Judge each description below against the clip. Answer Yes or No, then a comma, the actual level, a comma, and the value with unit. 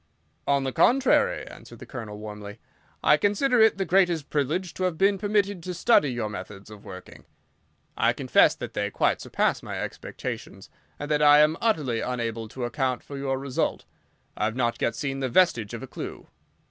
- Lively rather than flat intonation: Yes, wide, 7.5 semitones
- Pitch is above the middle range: No, medium, 140 Hz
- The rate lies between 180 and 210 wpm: Yes, average, 185 wpm